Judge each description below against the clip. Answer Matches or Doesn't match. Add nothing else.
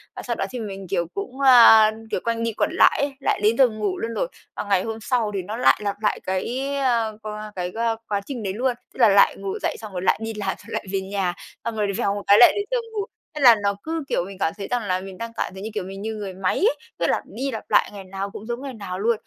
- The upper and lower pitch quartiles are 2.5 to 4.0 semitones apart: Matches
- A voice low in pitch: Doesn't match